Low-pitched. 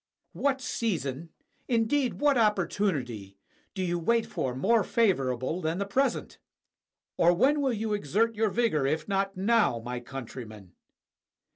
No: high, 195 Hz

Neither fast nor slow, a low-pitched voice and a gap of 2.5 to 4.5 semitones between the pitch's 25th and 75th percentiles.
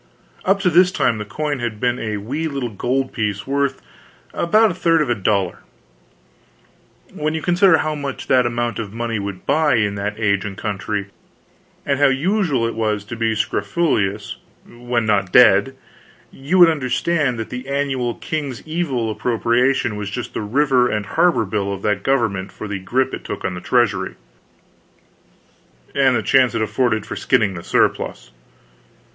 No: average, 170 wpm; low, 120 Hz; average, 5.1 semitones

